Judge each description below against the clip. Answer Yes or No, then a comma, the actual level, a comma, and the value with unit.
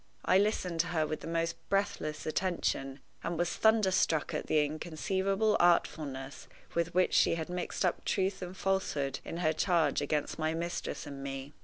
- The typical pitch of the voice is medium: Yes, medium, 170 Hz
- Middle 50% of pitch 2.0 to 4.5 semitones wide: Yes, average, 3.3 semitones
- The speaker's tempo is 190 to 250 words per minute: No, average, 170 wpm